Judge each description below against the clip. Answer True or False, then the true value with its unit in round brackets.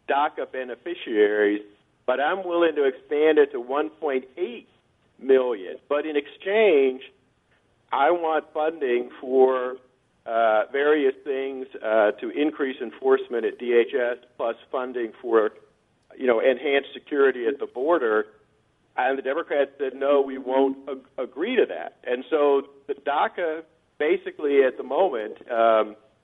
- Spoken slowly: True (130 wpm)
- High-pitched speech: False (145 Hz)